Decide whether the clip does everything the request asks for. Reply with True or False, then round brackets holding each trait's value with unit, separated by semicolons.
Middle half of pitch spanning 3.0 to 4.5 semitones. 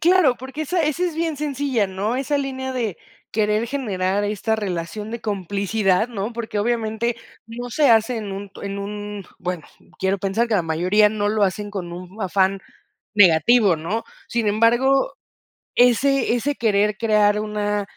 True (3.5 semitones)